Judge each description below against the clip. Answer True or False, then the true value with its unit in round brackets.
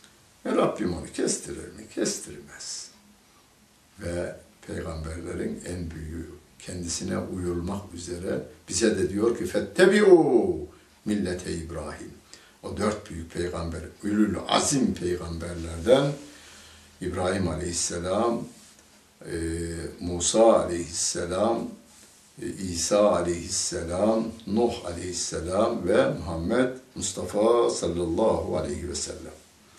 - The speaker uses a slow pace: True (85 wpm)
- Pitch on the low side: True (90 Hz)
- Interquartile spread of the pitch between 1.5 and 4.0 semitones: True (3.7 semitones)